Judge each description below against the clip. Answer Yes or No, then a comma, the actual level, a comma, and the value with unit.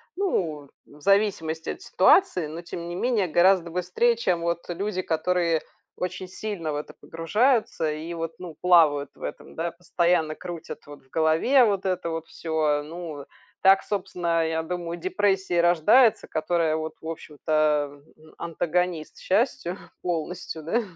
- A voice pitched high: No, medium, 170 Hz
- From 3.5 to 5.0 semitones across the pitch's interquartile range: No, average, 2.7 semitones